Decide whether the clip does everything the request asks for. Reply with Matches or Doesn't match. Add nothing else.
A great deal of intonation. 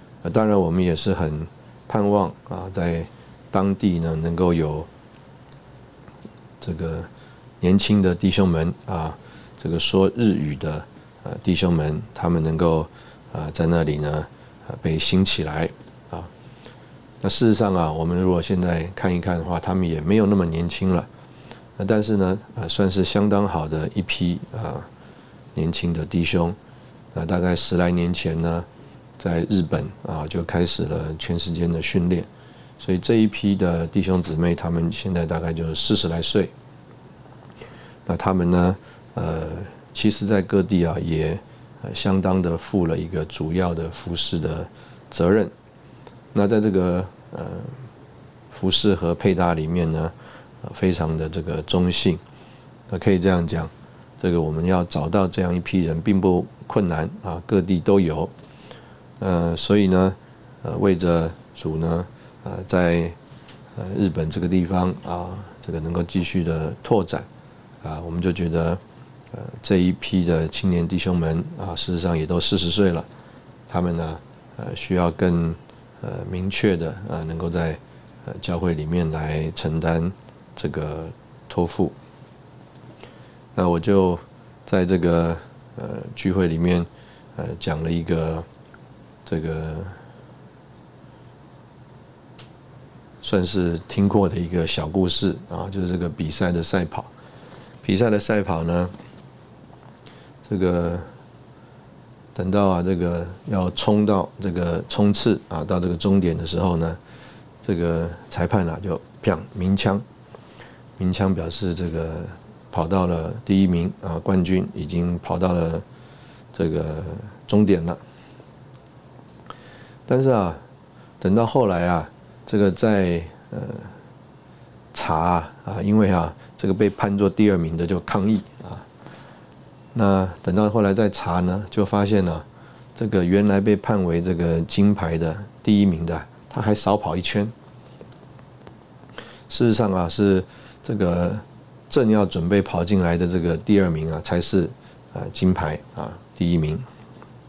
Doesn't match